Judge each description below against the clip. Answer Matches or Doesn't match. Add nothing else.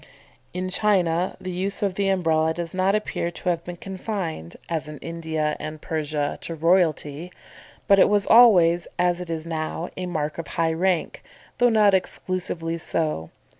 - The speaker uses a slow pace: Doesn't match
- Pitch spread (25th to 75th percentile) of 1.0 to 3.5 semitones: Matches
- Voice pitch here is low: Doesn't match